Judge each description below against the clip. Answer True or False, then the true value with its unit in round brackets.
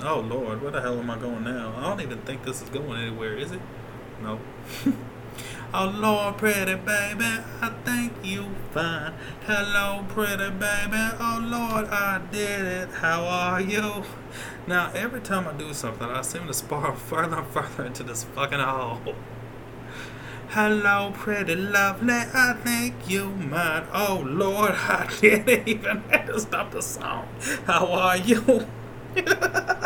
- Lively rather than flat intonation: True (8.2 semitones)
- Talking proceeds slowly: False (155 wpm)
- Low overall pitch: False (180 Hz)